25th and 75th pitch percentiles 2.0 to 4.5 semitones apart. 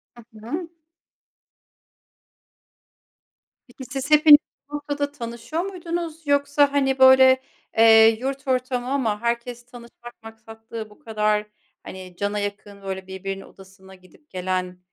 No: average, 5.1 semitones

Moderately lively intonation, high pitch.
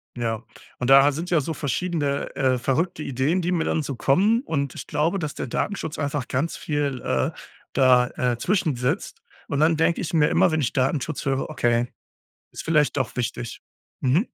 No: average, 4.0 semitones; medium, 145 Hz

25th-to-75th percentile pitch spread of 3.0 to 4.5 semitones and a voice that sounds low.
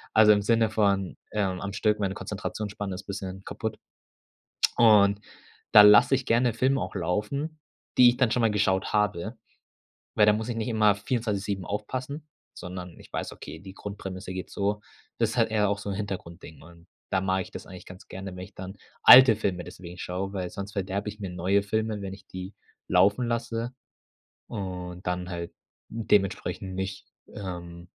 No: narrow, 2.6 semitones; low, 100 Hz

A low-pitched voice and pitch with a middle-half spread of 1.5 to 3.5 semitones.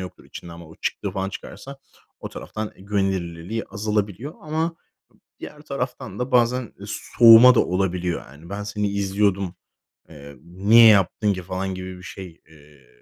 No: low, 100 Hz; average, 4.0 semitones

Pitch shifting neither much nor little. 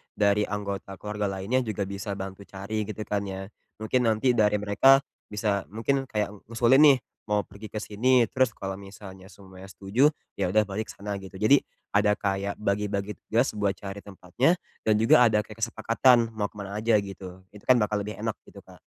No: narrow, 2.2 semitones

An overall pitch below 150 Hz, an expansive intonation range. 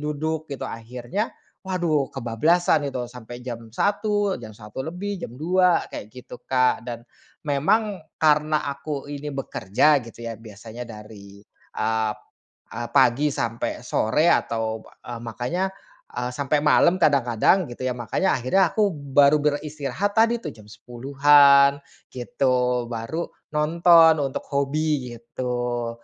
No: medium, 140 Hz; average, 4.7 semitones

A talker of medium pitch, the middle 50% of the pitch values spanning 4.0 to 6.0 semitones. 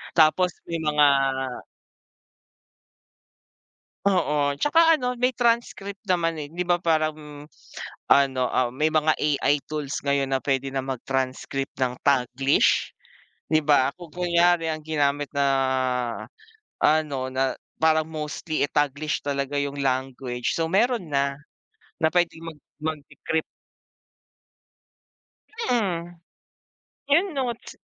No: medium, 150 Hz; average, 3.5 semitones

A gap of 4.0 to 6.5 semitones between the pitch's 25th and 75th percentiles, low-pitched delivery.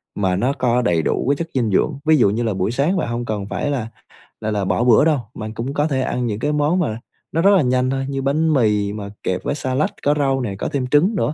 Yes: average, 5.1 semitones; low, 130 Hz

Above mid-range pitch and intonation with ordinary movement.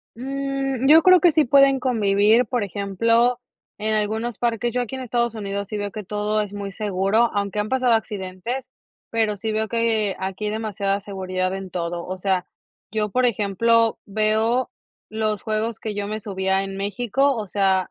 Yes: high, 215 Hz; average, 3.1 semitones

